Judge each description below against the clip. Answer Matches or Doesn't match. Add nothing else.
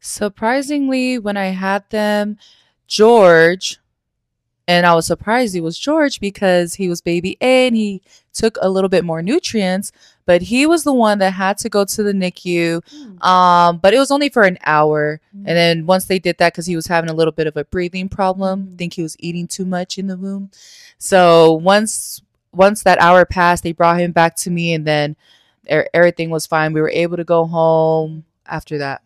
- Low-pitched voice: Doesn't match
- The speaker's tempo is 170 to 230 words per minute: Matches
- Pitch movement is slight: Doesn't match